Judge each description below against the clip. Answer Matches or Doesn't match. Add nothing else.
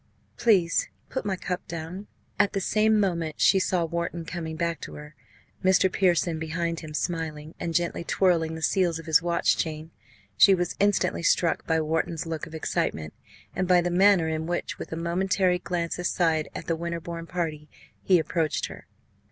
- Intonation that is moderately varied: Doesn't match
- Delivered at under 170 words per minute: Doesn't match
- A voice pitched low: Doesn't match